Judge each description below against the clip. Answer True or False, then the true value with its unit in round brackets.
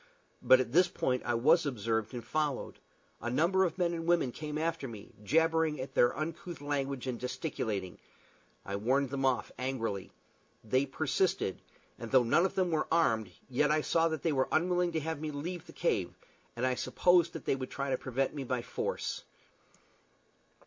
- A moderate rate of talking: True (185 wpm)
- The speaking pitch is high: False (140 Hz)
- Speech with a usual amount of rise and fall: True (4.5 semitones)